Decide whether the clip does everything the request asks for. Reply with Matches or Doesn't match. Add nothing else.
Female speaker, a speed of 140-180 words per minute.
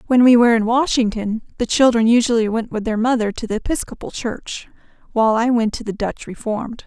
Doesn't match